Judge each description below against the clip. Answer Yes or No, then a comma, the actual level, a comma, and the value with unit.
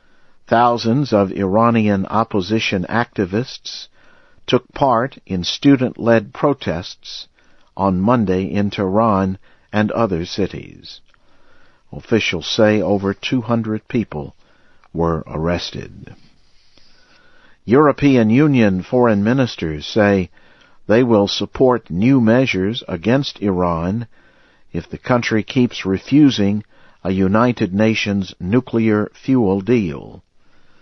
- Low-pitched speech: Yes, low, 105 Hz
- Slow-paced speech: Yes, slow, 90 wpm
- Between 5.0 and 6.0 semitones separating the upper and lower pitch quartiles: No, average, 3.8 semitones